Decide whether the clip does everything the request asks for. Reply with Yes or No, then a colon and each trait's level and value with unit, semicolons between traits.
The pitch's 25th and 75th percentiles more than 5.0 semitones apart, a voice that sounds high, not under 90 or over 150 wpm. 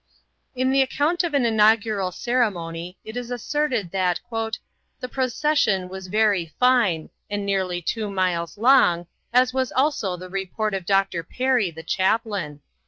Yes: wide, 5.5 semitones; high, 205 Hz; average, 145 wpm